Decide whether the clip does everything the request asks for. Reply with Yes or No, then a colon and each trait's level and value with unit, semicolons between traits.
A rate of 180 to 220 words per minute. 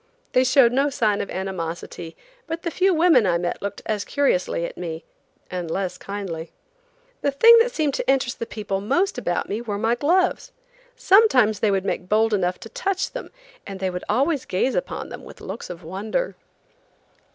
Yes: average, 185 wpm